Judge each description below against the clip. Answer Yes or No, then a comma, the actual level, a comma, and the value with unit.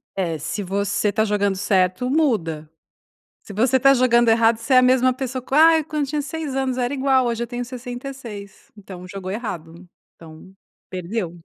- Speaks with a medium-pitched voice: No, high, 235 Hz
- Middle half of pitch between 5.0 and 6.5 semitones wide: Yes, average, 5.3 semitones